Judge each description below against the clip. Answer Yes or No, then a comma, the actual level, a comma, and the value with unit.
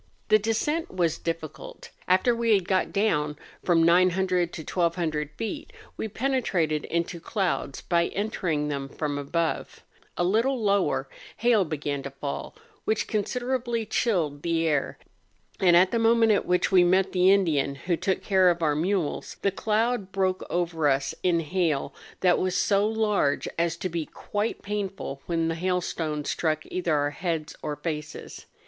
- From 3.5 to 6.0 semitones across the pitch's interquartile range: Yes, average, 4.3 semitones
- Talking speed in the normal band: Yes, average, 160 wpm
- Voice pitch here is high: No, medium, 180 Hz